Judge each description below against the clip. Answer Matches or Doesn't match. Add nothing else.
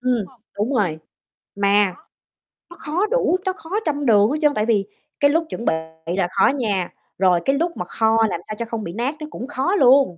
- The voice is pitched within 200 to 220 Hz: Doesn't match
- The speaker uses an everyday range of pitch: Doesn't match